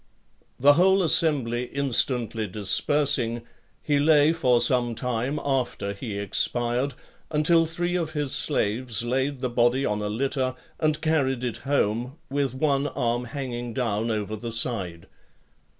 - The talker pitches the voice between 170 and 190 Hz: No, low, 125 Hz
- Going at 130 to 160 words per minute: Yes, average, 140 wpm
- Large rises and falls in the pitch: No, average, 3.8 semitones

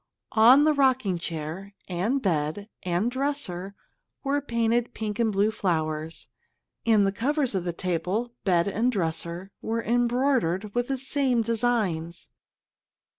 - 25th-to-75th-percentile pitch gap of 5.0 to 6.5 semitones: Yes, wide, 5.5 semitones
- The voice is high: Yes, high, 215 Hz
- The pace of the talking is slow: Yes, slow, 130 wpm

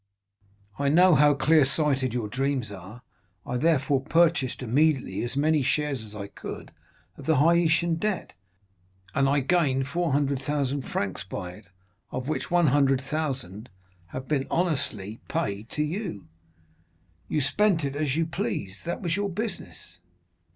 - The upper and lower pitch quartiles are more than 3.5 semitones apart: Yes, average, 4.1 semitones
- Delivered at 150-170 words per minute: No, average, 140 wpm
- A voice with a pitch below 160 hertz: Yes, medium, 140 Hz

